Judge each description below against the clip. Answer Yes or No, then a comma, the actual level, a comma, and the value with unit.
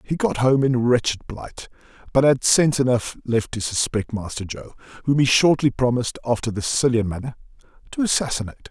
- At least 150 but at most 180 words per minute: Yes, average, 170 wpm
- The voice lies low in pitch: Yes, low, 125 Hz